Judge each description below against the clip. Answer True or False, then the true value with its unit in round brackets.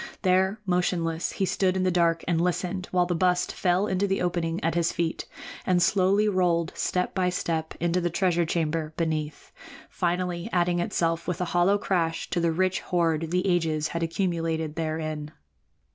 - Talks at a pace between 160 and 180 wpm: True (175 wpm)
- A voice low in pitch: False (175 Hz)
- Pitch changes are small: True (1.8 semitones)